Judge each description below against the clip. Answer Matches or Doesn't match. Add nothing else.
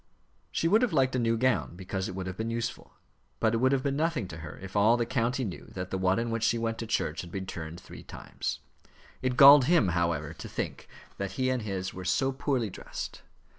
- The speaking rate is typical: Doesn't match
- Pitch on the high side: Doesn't match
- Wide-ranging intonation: Matches